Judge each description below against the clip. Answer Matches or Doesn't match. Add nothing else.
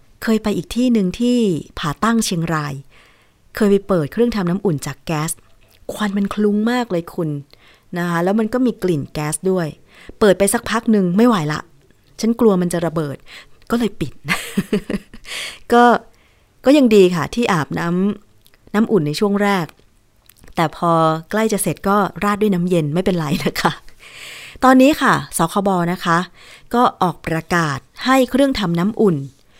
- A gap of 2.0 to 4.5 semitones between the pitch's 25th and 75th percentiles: Doesn't match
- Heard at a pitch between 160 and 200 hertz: Matches